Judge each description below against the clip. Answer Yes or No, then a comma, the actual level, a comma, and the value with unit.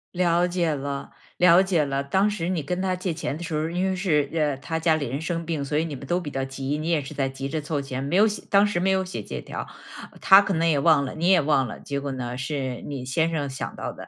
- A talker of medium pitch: Yes, medium, 155 Hz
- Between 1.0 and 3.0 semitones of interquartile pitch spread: No, average, 4.2 semitones